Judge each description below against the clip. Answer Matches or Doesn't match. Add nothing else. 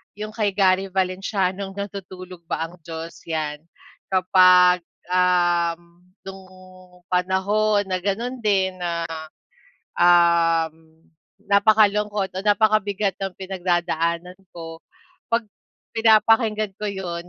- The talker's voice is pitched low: Doesn't match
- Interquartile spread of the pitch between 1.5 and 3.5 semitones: Matches